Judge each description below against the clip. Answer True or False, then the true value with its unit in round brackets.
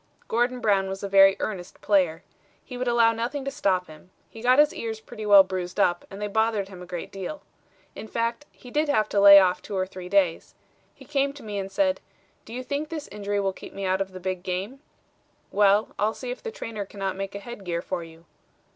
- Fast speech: True (235 wpm)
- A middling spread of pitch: True (4.0 semitones)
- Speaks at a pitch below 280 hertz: True (200 Hz)